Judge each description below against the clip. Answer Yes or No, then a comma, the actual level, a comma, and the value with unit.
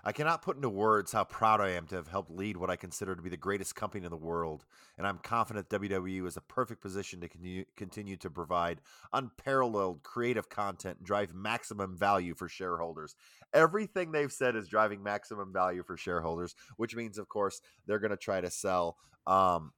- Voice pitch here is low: Yes, low, 100 Hz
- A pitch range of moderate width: Yes, average, 3.3 semitones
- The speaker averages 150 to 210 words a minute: Yes, average, 200 wpm